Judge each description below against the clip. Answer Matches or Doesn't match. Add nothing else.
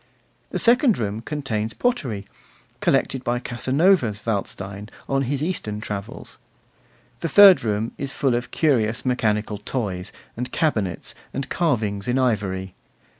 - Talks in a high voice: Doesn't match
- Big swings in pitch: Doesn't match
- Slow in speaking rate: Matches